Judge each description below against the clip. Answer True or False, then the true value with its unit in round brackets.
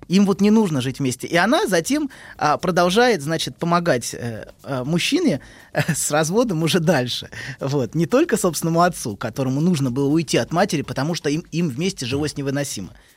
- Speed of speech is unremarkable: False (180 wpm)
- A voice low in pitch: False (155 Hz)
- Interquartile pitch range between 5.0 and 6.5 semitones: True (5.3 semitones)